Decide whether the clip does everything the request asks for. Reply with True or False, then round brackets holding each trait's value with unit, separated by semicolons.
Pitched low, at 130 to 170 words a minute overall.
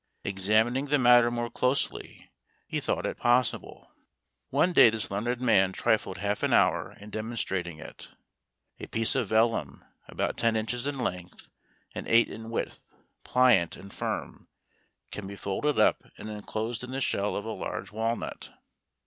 True (115 Hz; 155 wpm)